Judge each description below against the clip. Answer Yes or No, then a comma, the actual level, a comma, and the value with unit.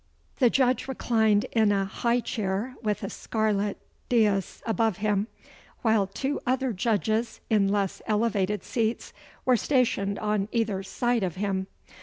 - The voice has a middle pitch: No, high, 215 Hz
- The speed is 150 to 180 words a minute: No, average, 140 wpm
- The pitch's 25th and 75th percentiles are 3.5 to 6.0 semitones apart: No, average, 2.9 semitones